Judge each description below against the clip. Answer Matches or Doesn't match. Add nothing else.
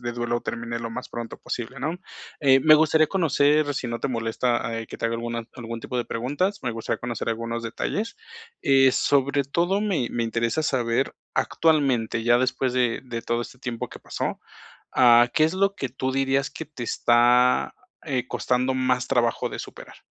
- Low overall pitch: Matches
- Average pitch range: Matches